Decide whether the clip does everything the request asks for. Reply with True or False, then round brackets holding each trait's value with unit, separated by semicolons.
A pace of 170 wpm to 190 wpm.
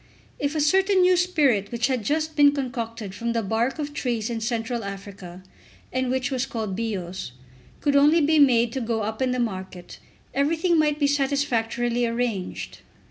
True (175 wpm)